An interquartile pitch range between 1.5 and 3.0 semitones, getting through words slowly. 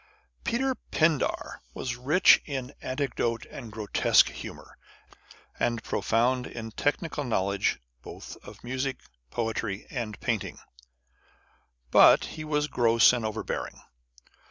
No: average, 4.1 semitones; slow, 110 wpm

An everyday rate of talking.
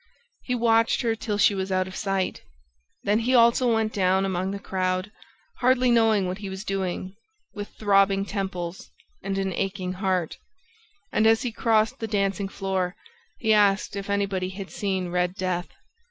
Yes: average, 170 wpm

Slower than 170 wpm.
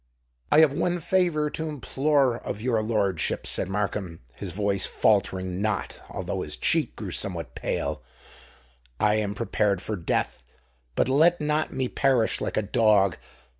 Yes: average, 145 wpm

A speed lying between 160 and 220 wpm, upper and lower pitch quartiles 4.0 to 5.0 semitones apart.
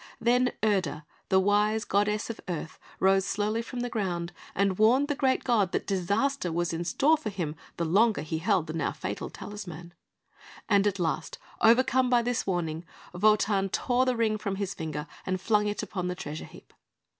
Yes: average, 185 wpm; average, 4.4 semitones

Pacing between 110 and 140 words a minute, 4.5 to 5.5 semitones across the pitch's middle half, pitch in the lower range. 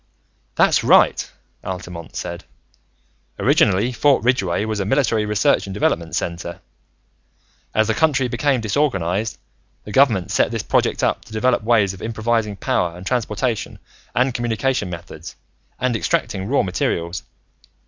Yes: slow, 135 wpm; average, 5.0 semitones; low, 110 Hz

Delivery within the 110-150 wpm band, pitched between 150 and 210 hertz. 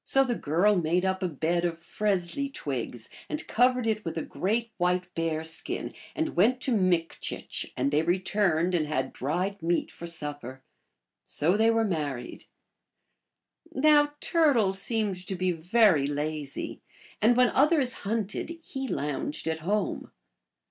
Yes: average, 145 wpm; medium, 185 Hz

